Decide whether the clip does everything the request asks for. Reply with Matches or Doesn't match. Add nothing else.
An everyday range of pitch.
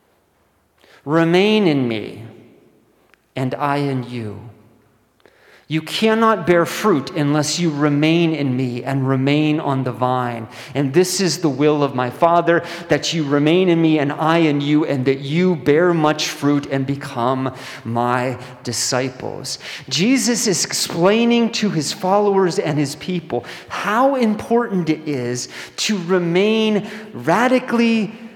Doesn't match